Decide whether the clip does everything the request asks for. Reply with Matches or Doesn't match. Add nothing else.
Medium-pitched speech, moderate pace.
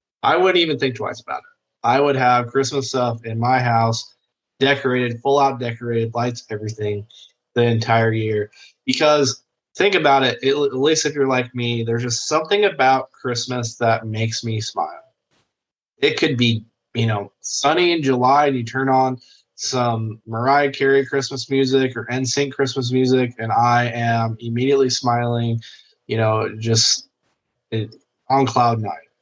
Doesn't match